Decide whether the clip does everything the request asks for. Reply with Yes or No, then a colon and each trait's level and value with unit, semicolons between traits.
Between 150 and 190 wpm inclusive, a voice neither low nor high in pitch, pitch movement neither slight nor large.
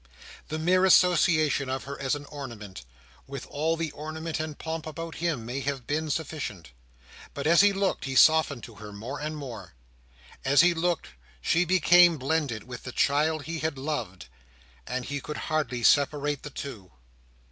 Yes: average, 170 wpm; medium, 145 Hz; average, 3.3 semitones